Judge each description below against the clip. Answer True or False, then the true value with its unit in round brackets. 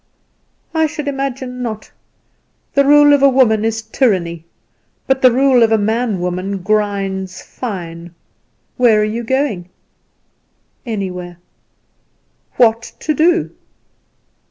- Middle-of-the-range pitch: False (225 Hz)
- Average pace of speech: False (115 wpm)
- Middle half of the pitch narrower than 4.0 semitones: False (5.4 semitones)